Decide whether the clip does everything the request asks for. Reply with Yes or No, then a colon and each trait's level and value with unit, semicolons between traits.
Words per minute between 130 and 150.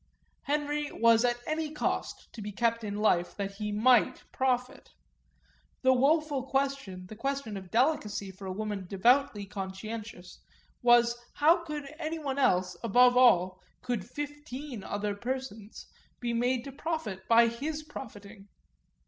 Yes: average, 140 wpm